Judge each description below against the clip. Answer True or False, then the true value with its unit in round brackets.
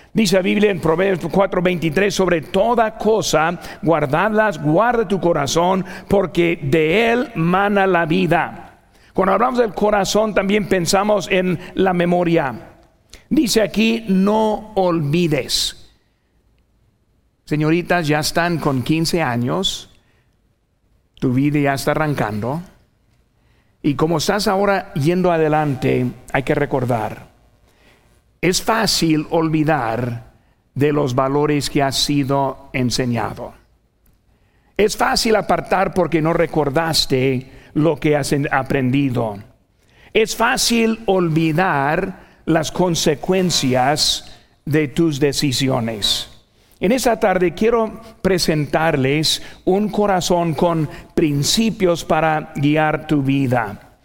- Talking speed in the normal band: False (105 wpm)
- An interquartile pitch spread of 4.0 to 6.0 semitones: True (5.1 semitones)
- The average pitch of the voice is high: False (165 Hz)